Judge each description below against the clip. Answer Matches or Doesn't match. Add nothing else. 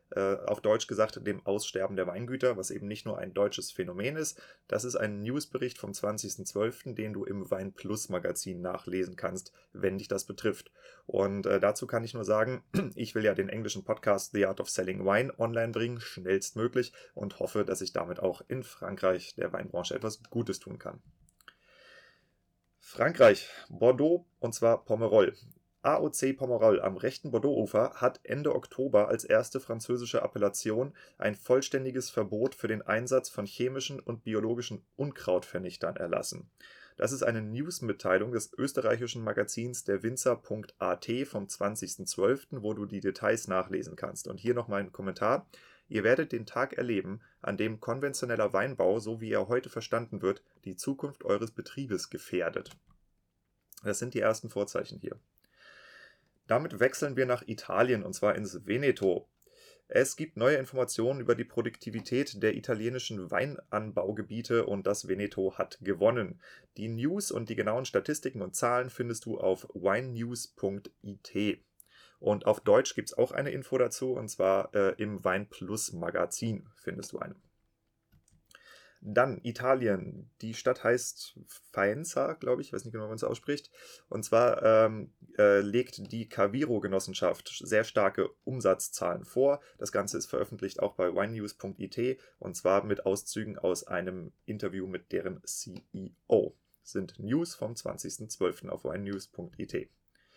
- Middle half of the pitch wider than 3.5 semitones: Matches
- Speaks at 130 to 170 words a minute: Matches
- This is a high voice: Doesn't match